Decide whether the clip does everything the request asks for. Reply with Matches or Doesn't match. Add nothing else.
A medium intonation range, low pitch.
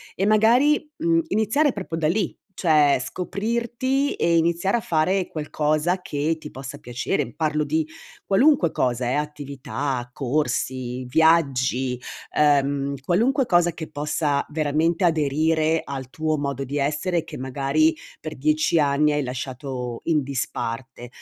Doesn't match